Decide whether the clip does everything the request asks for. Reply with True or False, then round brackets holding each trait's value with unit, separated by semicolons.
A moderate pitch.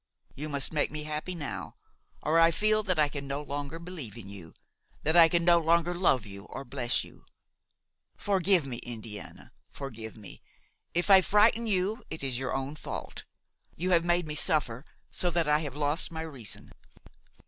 True (155 Hz)